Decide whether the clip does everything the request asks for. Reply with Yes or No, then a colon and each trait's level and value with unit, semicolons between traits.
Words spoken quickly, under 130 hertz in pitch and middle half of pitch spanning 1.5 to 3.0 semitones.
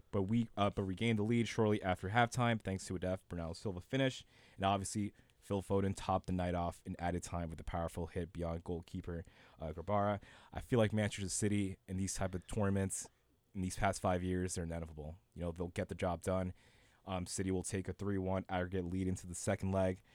Yes: fast, 215 wpm; very low, 95 Hz; narrow, 2.4 semitones